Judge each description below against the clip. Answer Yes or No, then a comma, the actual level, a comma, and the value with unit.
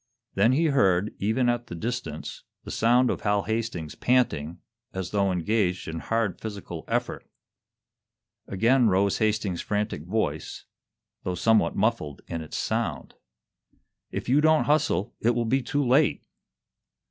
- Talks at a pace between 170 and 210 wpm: No, average, 140 wpm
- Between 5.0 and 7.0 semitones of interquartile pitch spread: No, average, 4.6 semitones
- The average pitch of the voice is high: No, low, 110 Hz